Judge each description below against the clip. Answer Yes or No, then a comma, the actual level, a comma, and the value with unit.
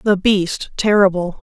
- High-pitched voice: Yes, high, 195 Hz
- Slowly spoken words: Yes, slow, 120 wpm